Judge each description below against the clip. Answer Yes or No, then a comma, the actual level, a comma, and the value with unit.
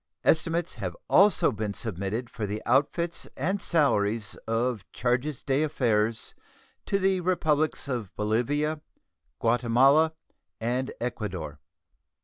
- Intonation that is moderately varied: No, wide, 6.0 semitones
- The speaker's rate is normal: No, slow, 105 wpm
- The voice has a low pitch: Yes, low, 125 Hz